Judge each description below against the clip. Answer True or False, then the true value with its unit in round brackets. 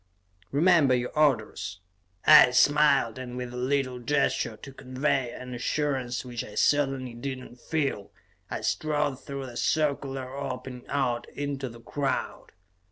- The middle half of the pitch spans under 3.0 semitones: True (2.4 semitones)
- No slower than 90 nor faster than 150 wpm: True (140 wpm)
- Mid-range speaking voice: False (130 Hz)